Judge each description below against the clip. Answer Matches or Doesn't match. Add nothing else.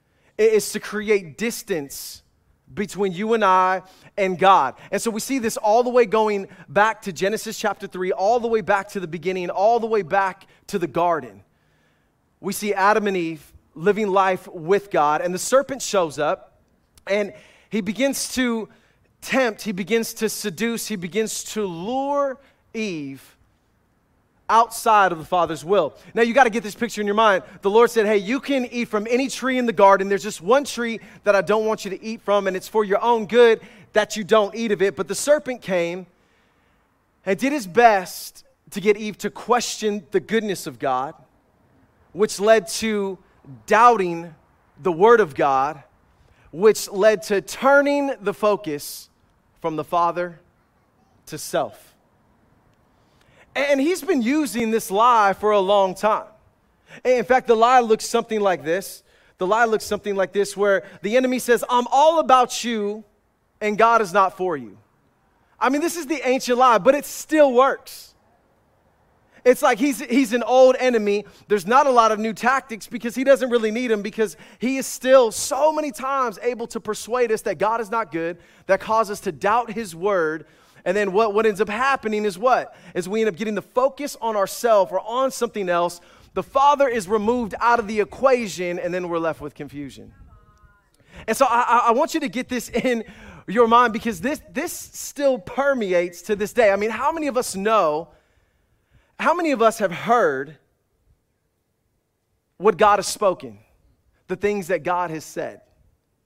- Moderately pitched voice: Doesn't match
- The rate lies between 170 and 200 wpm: Matches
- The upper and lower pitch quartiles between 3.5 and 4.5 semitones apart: Matches